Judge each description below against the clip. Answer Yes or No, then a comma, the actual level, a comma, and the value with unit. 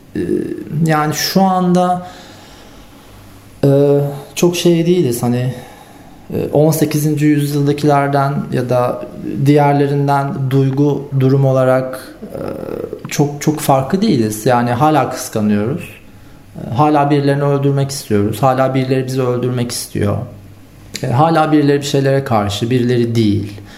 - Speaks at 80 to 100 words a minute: Yes, slow, 95 wpm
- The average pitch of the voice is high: No, medium, 140 Hz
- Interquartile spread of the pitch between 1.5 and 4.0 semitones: Yes, average, 3.4 semitones